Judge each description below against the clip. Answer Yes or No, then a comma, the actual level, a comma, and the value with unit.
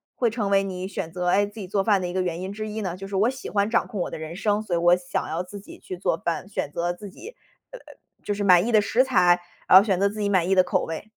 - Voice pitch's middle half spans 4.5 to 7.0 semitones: No, average, 2.8 semitones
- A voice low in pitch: No, high, 195 Hz